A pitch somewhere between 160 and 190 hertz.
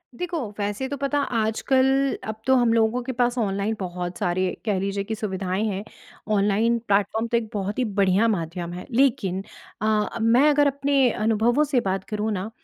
No: high, 220 Hz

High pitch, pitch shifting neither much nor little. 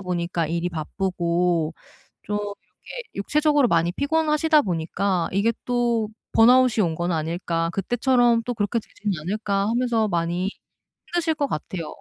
No: high, 200 Hz; wide, 6.0 semitones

